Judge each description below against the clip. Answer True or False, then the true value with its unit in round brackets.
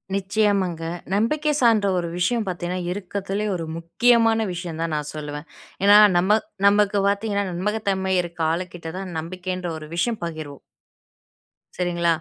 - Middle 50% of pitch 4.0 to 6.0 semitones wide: False (3.4 semitones)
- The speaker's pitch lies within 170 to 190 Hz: True (185 Hz)